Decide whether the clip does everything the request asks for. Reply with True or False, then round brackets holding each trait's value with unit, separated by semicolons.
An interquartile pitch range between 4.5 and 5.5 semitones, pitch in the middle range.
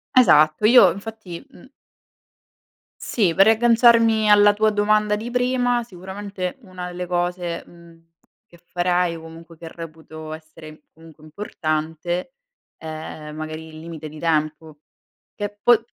True (4.8 semitones; 175 Hz)